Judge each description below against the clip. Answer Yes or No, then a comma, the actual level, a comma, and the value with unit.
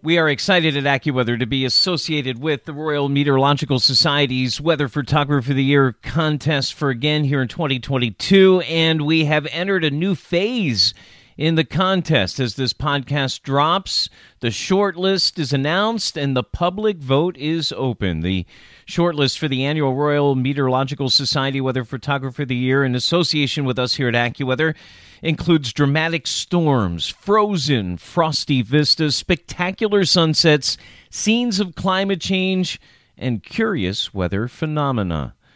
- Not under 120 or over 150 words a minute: Yes, average, 140 wpm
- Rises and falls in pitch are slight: No, average, 3.9 semitones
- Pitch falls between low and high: Yes, medium, 145 Hz